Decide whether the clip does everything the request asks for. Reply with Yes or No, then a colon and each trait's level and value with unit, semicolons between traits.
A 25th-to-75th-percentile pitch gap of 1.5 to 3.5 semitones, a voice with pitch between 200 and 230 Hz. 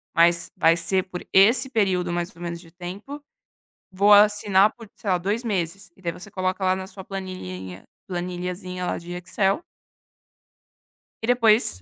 No: narrow, 2.6 semitones; medium, 185 Hz